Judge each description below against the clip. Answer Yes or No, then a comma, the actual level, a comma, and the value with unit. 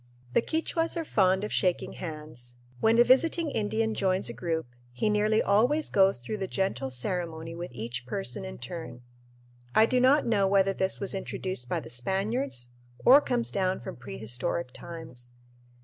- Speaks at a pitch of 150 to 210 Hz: Yes, high, 190 Hz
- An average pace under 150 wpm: No, average, 165 wpm